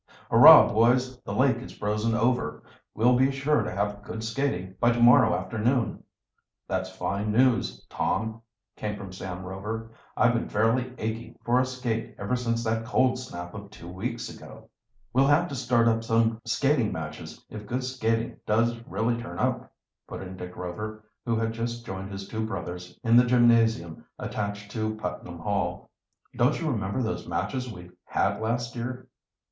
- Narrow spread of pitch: No, average, 3.2 semitones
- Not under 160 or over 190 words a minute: Yes, average, 170 wpm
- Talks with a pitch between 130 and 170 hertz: No, low, 115 Hz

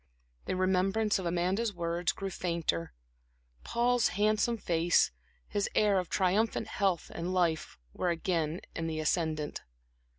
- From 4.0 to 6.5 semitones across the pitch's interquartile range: No, average, 3.2 semitones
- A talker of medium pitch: Yes, medium, 180 Hz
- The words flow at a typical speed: No, slow, 130 wpm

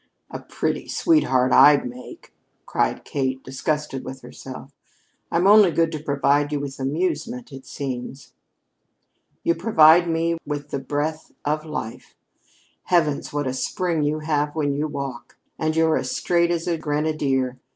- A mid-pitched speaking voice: Yes, medium, 150 Hz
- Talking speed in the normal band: Yes, average, 150 wpm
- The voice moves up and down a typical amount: Yes, average, 3.1 semitones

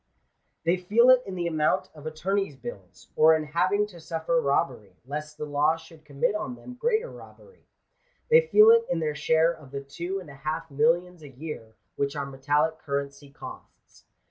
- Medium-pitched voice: Yes, medium, 160 Hz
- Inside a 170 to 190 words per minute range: Yes, average, 185 wpm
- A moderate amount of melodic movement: Yes, average, 4.3 semitones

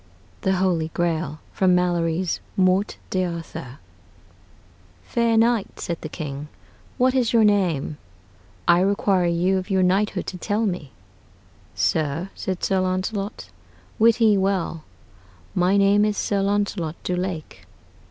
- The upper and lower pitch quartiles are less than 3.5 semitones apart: Yes, average, 3.1 semitones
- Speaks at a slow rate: Yes, slow, 130 wpm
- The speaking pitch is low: No, medium, 185 Hz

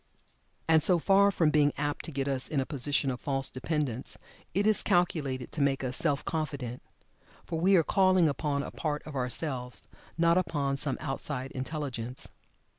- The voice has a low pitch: No, medium, 145 Hz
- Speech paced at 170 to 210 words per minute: Yes, average, 175 wpm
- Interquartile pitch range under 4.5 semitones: Yes, average, 3.5 semitones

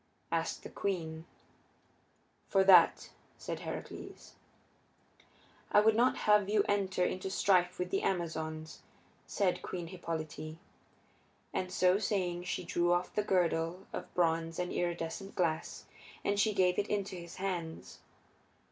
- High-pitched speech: No, medium, 180 Hz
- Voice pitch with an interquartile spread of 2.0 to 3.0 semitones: Yes, narrow, 2.6 semitones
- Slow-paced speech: Yes, slow, 130 wpm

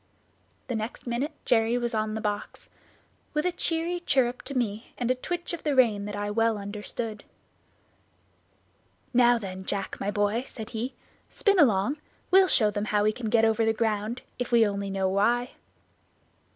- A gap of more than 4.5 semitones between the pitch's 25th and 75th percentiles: No, average, 3.2 semitones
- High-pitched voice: Yes, high, 225 Hz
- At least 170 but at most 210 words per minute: Yes, average, 175 wpm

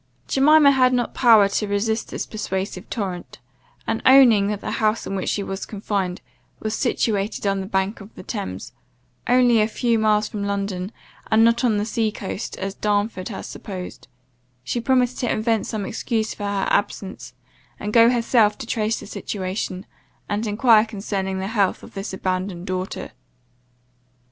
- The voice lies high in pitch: Yes, high, 210 Hz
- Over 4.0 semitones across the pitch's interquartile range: No, average, 2.7 semitones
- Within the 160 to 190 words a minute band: Yes, average, 170 wpm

